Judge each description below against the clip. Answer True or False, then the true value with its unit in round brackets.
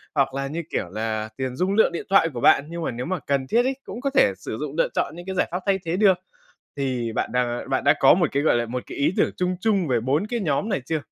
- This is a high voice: False (150 Hz)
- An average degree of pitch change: False (6.6 semitones)